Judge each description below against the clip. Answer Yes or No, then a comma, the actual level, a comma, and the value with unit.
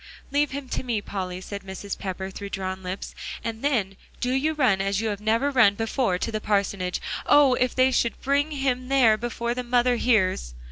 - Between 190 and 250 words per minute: Yes, average, 200 wpm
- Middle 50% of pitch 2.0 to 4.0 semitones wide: No, average, 4.8 semitones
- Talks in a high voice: Yes, high, 225 Hz